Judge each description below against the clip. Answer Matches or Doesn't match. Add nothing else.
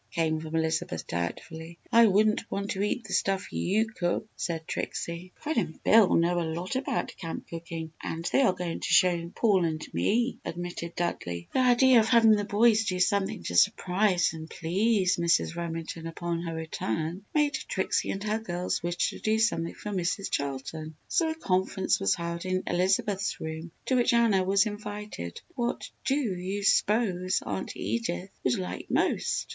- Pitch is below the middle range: Doesn't match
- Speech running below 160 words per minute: Doesn't match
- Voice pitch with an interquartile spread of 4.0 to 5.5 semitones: Matches